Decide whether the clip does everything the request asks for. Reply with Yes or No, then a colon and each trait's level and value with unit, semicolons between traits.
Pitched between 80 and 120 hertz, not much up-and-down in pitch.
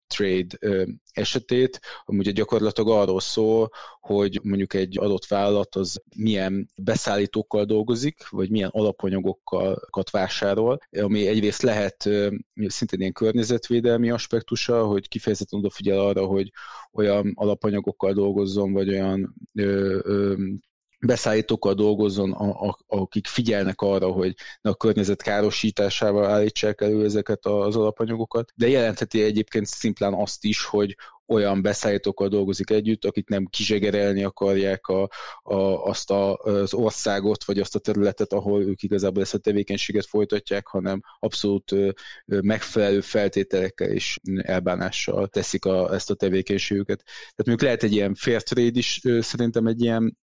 Yes: low, 100 Hz; narrow, 1.6 semitones